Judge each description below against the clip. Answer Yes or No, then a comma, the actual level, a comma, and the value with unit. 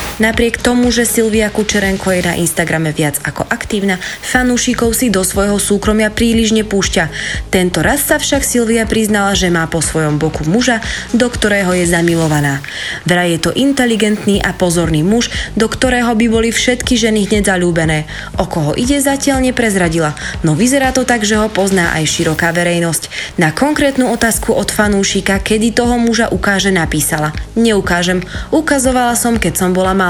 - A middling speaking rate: Yes, average, 160 wpm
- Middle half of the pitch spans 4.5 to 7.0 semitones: Yes, average, 5.2 semitones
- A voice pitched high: Yes, high, 200 Hz